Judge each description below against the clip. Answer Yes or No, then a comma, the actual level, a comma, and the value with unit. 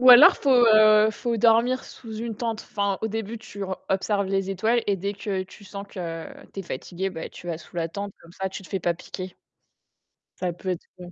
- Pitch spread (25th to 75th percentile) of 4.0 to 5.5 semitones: No, average, 3.0 semitones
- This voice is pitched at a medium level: No, high, 200 Hz